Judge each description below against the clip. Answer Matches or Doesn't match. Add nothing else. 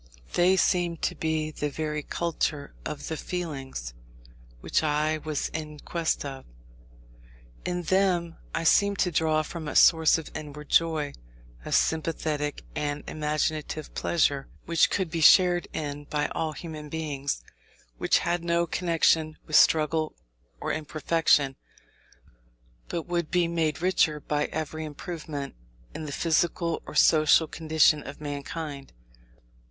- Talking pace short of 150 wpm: Matches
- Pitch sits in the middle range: Matches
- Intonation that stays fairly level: Matches